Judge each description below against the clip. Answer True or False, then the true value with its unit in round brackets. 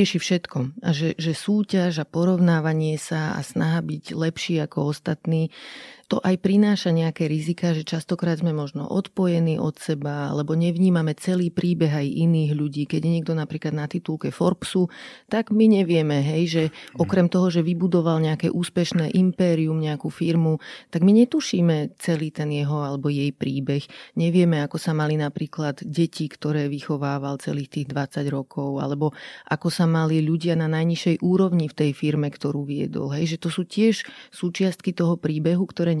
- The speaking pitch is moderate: True (165 Hz)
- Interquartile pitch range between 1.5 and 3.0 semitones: True (2.7 semitones)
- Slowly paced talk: False (160 wpm)